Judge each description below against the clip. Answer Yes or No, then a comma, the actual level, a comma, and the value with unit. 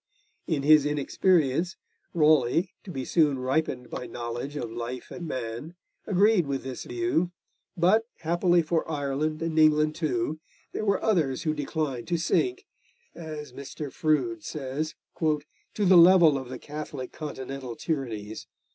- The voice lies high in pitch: No, medium, 155 Hz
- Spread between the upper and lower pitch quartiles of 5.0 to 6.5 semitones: No, average, 4.3 semitones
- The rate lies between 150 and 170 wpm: No, average, 140 wpm